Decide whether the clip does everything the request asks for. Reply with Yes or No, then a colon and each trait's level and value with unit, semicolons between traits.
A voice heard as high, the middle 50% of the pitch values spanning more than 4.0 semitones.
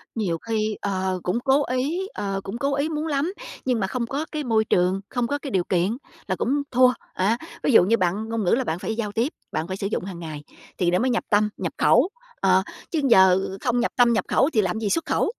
Yes: high, 220 Hz; average, 5.3 semitones